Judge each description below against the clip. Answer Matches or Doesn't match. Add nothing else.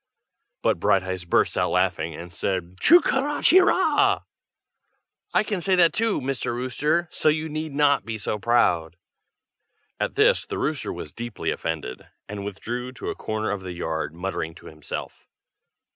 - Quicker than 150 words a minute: Matches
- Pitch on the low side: Matches